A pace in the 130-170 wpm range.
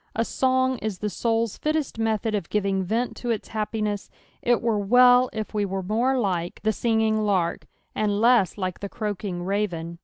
No: average, 180 wpm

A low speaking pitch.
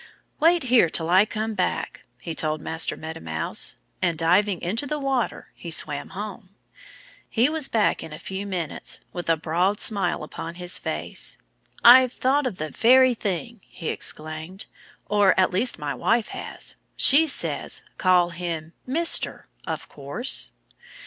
No: high, 190 Hz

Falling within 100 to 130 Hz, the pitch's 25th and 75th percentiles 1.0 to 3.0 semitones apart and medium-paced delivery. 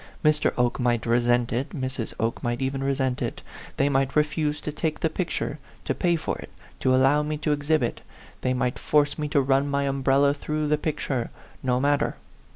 No: medium, 140 Hz; narrow, 2.6 semitones; average, 190 wpm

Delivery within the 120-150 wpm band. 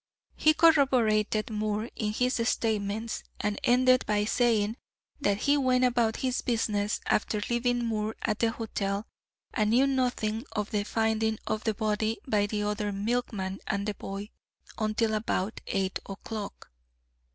Yes: average, 145 wpm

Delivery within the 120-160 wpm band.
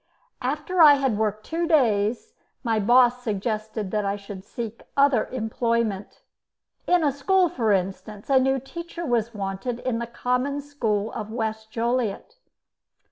Yes: average, 145 wpm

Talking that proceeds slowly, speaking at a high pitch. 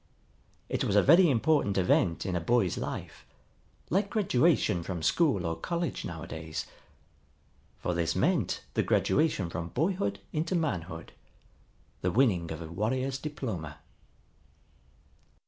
No: slow, 125 wpm; low, 105 Hz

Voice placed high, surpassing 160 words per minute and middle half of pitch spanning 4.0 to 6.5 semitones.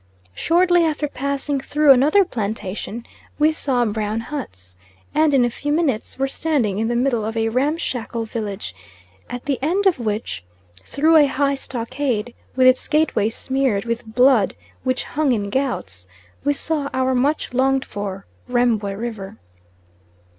No: very high, 255 Hz; average, 150 wpm; average, 4.5 semitones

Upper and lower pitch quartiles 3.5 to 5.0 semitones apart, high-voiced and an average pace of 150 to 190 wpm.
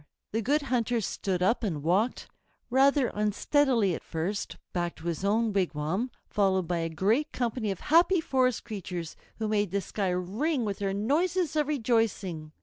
No: wide, 5.6 semitones; high, 210 Hz; average, 165 wpm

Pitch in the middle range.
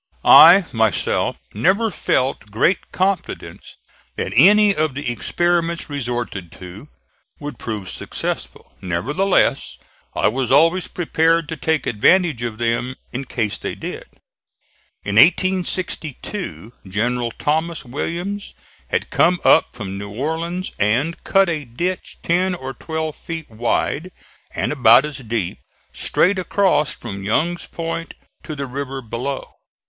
Yes: medium, 145 Hz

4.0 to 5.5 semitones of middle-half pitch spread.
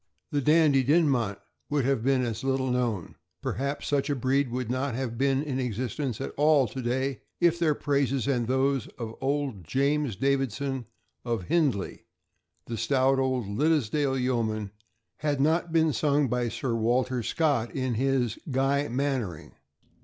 No: average, 2.8 semitones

